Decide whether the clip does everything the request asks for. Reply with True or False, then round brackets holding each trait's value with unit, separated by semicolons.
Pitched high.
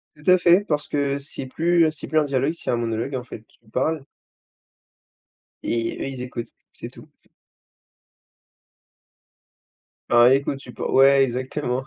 False (135 Hz)